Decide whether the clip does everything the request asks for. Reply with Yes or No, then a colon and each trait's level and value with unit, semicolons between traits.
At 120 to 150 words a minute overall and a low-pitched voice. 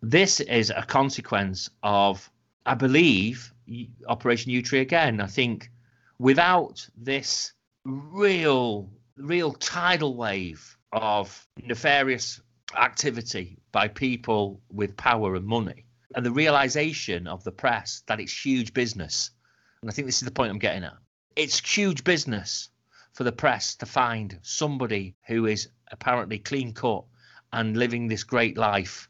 Yes: average, 140 wpm; low, 120 Hz